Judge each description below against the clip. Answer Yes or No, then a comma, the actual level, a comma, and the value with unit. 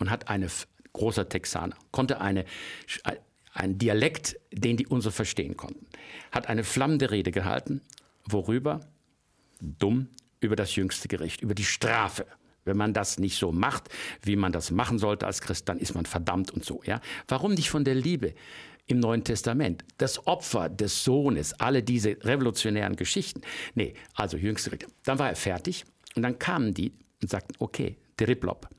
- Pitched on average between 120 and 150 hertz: No, low, 105 Hz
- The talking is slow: No, average, 175 wpm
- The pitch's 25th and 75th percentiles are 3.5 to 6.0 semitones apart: Yes, average, 4.6 semitones